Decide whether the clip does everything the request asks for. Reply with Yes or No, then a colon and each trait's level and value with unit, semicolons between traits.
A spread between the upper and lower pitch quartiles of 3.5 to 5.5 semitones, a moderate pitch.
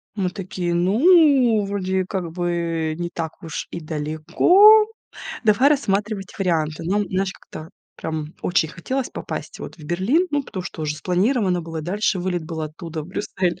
Yes: average, 4.1 semitones; medium, 180 Hz